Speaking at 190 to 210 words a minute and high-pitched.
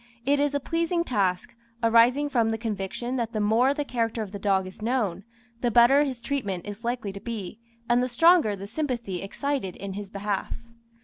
Yes: average, 195 wpm; high, 230 Hz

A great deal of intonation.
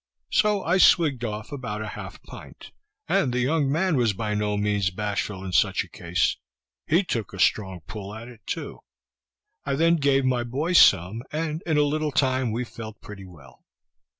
Yes: wide, 6.2 semitones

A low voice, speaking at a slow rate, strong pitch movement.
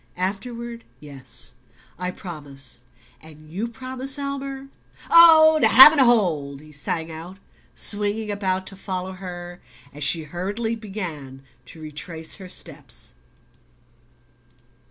No: medium, 185 Hz; slow, 120 wpm; wide, 6.9 semitones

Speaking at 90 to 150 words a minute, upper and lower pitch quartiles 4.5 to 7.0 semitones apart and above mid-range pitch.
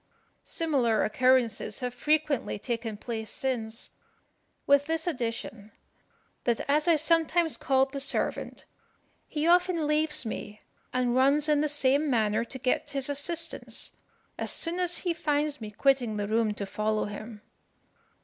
Yes: average, 140 wpm; average, 5.1 semitones; very high, 270 Hz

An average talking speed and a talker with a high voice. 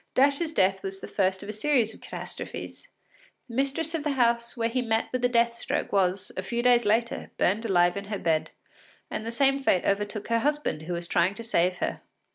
No: fast, 220 wpm; high, 225 Hz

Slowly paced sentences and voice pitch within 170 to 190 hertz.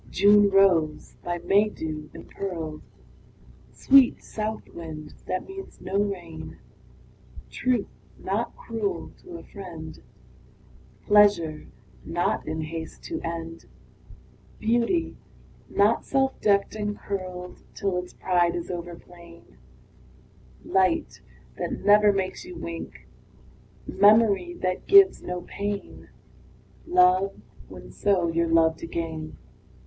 Yes: slow, 110 wpm; medium, 185 Hz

